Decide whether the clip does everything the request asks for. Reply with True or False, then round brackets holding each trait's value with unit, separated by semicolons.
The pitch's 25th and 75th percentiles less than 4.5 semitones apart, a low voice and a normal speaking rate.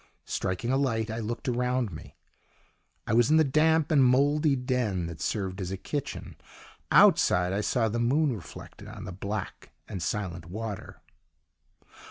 False (5.5 semitones; 115 Hz; 160 wpm)